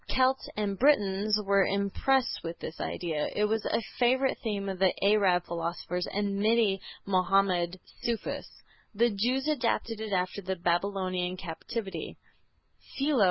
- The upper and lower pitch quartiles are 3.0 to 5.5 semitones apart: Yes, average, 3.3 semitones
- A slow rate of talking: Yes, slow, 130 wpm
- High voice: Yes, high, 200 Hz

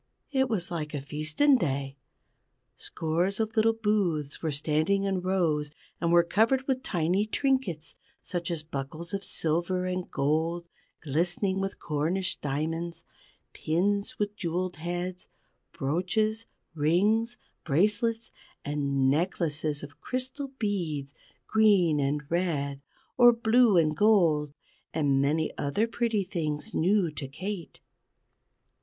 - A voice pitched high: No, medium, 175 Hz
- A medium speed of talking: No, slow, 120 wpm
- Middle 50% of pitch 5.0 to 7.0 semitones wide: Yes, average, 5.3 semitones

